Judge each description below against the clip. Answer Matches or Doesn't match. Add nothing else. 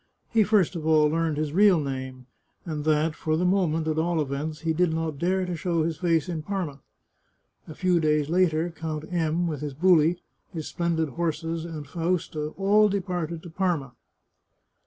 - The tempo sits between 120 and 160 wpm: Doesn't match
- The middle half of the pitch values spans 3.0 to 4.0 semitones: Doesn't match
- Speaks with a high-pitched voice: Doesn't match